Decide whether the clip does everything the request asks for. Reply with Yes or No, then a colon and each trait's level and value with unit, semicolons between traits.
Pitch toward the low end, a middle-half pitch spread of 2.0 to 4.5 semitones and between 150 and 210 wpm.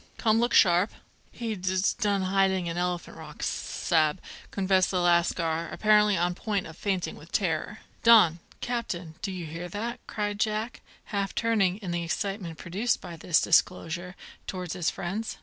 No: medium, 185 Hz; average, 3.4 semitones; average, 175 wpm